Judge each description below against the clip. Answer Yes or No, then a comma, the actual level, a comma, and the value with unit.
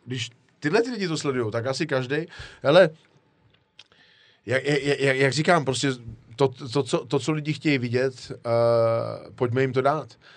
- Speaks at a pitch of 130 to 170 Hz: Yes, low, 135 Hz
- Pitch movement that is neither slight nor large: Yes, average, 3.2 semitones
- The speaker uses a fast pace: No, average, 160 wpm